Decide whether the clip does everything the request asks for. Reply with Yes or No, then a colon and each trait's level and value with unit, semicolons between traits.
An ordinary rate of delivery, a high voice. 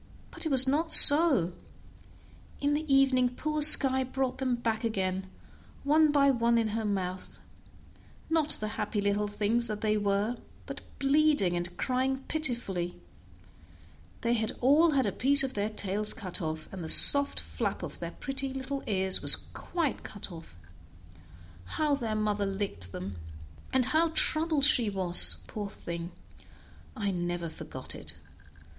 Yes: average, 150 wpm; high, 235 Hz